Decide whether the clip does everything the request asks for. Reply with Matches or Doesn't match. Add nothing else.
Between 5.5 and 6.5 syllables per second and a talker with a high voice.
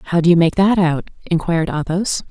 Doesn't match